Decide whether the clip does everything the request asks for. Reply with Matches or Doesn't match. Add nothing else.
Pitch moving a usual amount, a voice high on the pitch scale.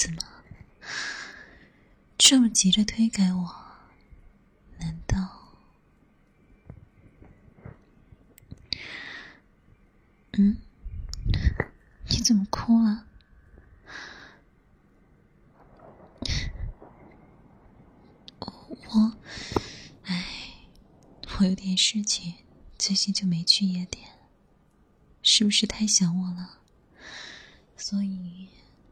Matches